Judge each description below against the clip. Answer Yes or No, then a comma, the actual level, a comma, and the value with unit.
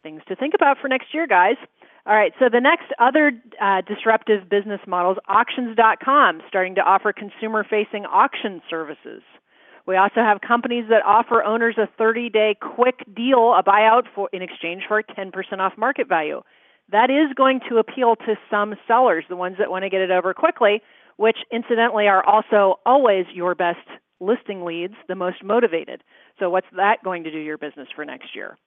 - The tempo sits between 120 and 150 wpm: No, average, 185 wpm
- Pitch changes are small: No, average, 3.7 semitones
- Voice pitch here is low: No, high, 210 Hz